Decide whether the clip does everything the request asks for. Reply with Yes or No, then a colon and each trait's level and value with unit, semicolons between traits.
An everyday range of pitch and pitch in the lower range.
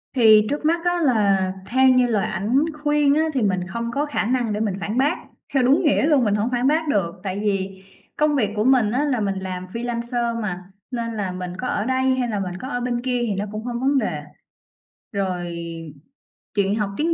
No: average, 4.6 semitones; high, 235 Hz